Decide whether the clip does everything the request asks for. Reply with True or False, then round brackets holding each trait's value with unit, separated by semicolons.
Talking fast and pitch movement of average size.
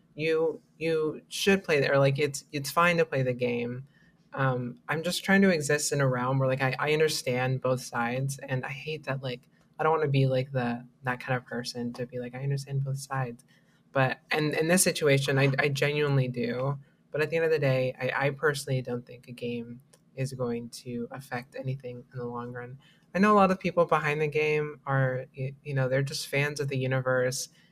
True (220 wpm; 3.1 semitones)